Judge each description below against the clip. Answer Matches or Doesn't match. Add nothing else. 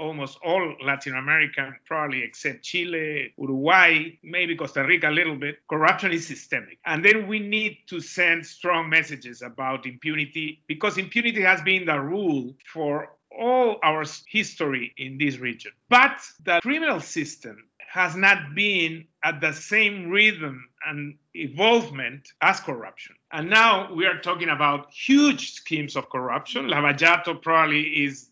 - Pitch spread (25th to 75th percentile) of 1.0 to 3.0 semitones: Doesn't match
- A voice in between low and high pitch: Matches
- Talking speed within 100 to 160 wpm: Matches